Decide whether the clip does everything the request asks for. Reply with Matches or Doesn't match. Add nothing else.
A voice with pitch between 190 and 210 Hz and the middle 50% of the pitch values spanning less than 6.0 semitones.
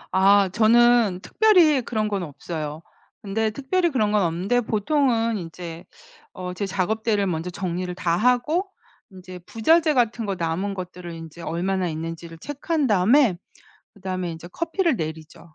Matches